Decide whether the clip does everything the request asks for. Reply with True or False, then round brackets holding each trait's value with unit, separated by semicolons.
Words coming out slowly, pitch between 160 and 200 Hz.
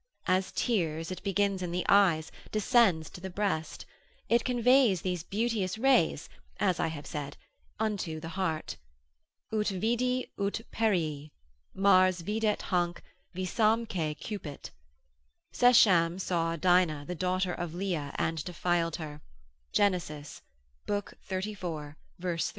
True (120 wpm; 185 Hz)